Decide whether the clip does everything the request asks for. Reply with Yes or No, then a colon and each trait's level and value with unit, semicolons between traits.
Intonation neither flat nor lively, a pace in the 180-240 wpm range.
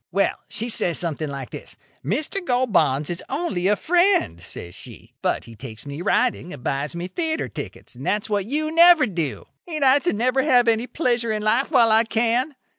No: wide, 8.0 semitones; average, 200 wpm